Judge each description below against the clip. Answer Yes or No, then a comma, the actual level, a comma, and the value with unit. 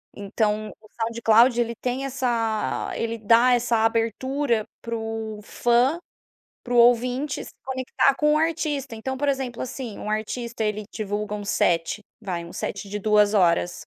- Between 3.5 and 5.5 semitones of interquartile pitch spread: No, average, 3.0 semitones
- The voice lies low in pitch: No, high, 230 Hz